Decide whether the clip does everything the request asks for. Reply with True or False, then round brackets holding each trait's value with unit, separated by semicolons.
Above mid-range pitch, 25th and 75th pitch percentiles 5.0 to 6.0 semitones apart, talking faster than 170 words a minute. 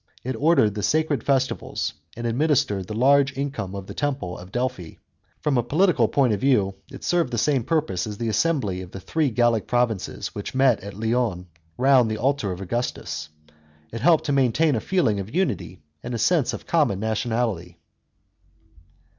False (120 Hz; 5.4 semitones; 180 wpm)